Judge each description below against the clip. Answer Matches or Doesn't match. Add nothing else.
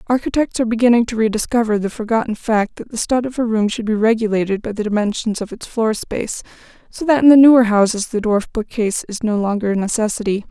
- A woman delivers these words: Matches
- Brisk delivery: Matches